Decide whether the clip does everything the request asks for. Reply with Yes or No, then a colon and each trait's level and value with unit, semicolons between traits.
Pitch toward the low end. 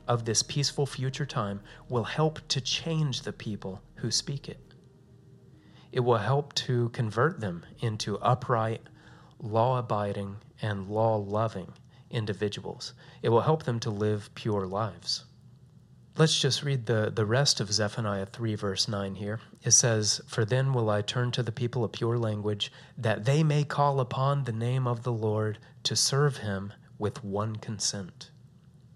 Yes: low, 120 Hz